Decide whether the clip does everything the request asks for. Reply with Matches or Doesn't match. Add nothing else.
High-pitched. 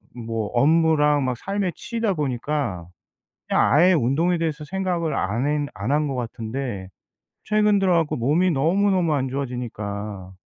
Doesn't match